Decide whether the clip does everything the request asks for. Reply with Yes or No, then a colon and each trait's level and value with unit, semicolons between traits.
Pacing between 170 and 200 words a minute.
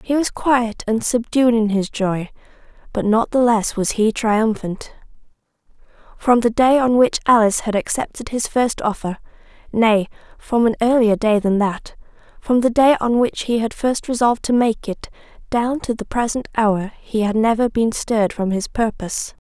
Yes: average, 175 wpm